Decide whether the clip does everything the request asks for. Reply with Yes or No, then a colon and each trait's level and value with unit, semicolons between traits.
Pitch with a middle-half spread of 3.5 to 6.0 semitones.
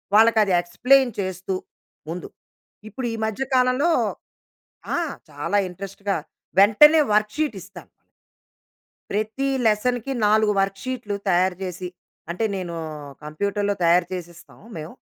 Yes: average, 4.2 semitones